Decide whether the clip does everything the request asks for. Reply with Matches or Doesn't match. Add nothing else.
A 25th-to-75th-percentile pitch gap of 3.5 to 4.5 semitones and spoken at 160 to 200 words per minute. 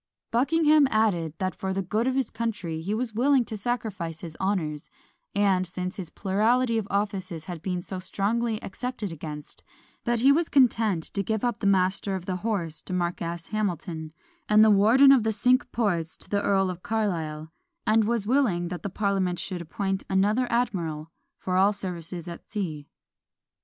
Matches